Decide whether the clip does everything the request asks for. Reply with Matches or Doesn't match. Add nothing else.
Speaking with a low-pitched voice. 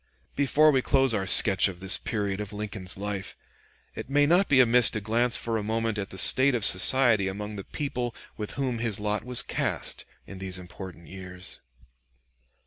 Matches